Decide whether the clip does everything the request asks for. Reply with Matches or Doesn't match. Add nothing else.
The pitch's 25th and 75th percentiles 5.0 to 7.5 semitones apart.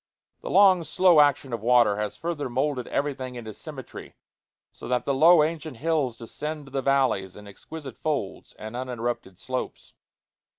Doesn't match